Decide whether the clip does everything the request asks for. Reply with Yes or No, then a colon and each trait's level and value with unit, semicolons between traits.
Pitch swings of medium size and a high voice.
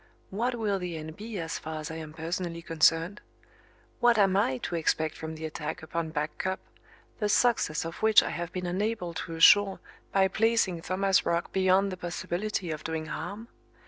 No: average, 3.7 semitones; medium, 175 Hz